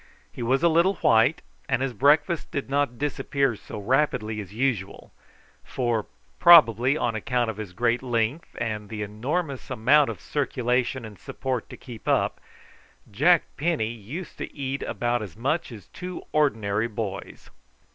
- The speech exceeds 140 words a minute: Yes, average, 155 wpm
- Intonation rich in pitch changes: No, average, 4.6 semitones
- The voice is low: Yes, low, 125 Hz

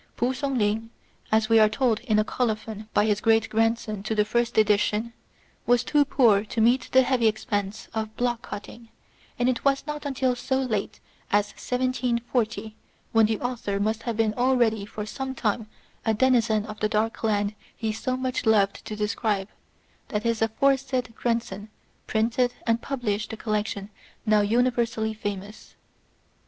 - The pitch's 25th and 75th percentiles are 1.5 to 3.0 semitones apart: Yes, narrow, 2.4 semitones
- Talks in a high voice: Yes, high, 225 Hz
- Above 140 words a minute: Yes, average, 165 wpm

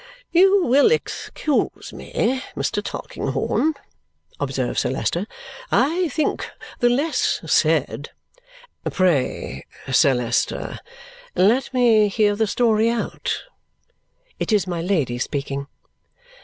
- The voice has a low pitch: No, high, 220 Hz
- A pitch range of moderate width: No, wide, 8.7 semitones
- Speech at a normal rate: No, slow, 105 wpm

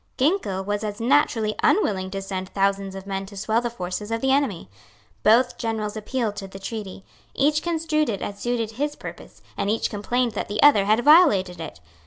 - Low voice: No, high, 215 Hz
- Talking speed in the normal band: Yes, average, 195 wpm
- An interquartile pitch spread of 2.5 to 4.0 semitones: No, average, 4.5 semitones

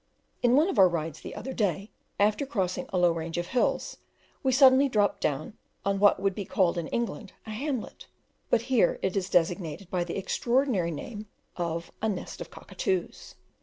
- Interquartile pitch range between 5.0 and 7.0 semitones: Yes, wide, 5.5 semitones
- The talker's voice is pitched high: Yes, high, 200 Hz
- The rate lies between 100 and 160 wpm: No, average, 185 wpm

